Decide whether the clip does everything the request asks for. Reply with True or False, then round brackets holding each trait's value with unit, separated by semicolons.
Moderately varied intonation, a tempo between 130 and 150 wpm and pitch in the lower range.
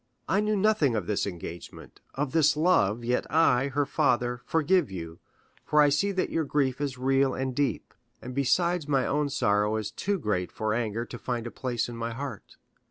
False (4.6 semitones; 195 wpm; 130 Hz)